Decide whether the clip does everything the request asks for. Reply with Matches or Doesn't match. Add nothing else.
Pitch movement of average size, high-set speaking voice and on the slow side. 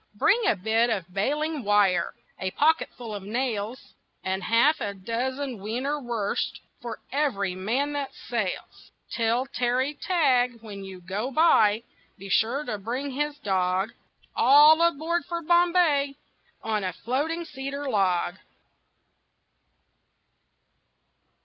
Doesn't match